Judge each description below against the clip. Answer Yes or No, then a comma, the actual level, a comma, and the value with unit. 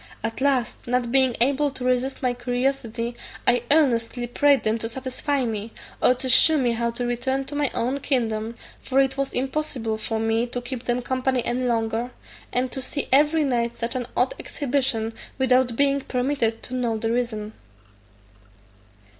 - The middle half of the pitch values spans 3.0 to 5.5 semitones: No, narrow, 2.4 semitones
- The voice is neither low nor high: No, very high, 250 Hz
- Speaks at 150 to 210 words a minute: Yes, average, 170 wpm